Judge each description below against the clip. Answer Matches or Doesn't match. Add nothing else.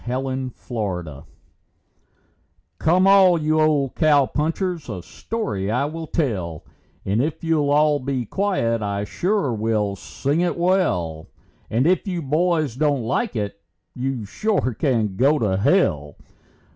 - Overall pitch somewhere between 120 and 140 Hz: Matches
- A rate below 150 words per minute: Matches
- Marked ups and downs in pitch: Matches